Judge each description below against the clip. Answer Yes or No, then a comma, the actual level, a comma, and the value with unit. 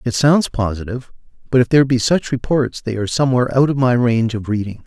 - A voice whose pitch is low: Yes, low, 125 Hz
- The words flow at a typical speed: No, fast, 220 wpm